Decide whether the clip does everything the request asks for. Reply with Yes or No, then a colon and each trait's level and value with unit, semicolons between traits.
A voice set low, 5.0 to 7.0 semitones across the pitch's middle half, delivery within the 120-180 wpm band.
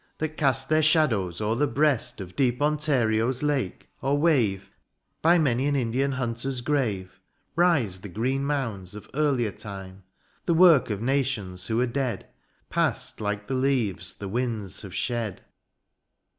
Yes: low, 125 Hz; average, 5.3 semitones; average, 160 wpm